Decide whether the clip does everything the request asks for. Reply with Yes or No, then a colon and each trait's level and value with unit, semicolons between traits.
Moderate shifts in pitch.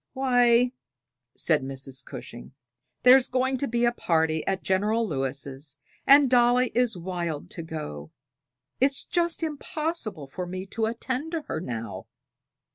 No: wide, 8.6 semitones